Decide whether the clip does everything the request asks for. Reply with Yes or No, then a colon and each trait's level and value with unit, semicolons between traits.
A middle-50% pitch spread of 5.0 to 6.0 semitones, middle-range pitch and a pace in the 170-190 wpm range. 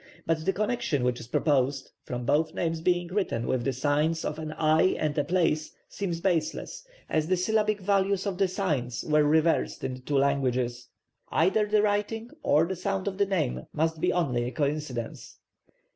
Yes: average, 5.3 semitones; medium, 160 Hz; average, 185 wpm